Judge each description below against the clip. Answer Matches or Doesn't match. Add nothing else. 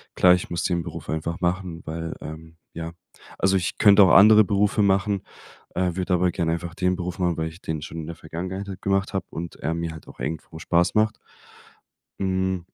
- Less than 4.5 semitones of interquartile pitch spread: Matches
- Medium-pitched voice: Doesn't match